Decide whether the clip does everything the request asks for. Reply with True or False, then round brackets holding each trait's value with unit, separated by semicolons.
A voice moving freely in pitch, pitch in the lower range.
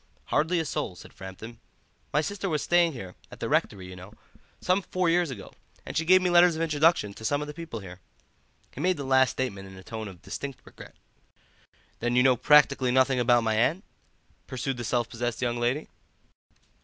True (6.2 semitones; 130 Hz)